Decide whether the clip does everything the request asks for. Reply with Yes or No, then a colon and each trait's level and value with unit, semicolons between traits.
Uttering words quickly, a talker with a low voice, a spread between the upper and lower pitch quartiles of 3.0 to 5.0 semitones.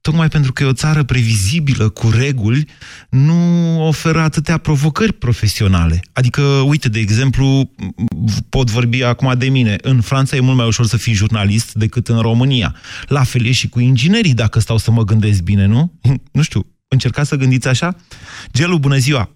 Yes: fast, 175 wpm; low, 125 Hz; average, 4.2 semitones